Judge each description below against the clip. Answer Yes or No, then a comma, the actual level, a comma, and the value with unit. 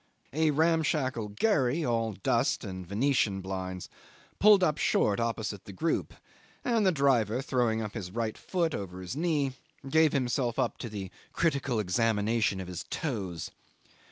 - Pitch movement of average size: No, wide, 6.7 semitones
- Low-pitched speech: Yes, low, 120 Hz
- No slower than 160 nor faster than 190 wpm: No, average, 150 wpm